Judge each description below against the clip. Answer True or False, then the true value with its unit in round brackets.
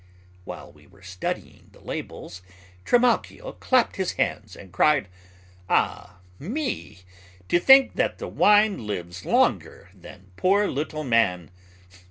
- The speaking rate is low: True (120 wpm)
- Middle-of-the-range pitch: True (145 Hz)